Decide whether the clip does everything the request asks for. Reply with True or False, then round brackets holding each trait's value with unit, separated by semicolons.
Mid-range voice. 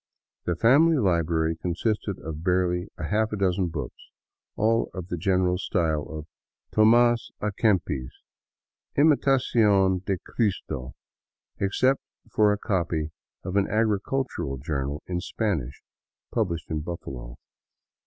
False (95 Hz)